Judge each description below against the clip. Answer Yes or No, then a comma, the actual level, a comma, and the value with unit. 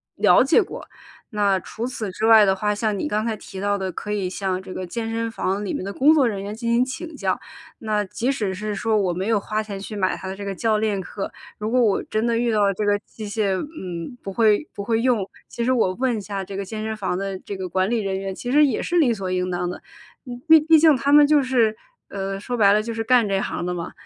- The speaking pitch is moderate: No, high, 210 Hz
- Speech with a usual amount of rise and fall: Yes, average, 3.3 semitones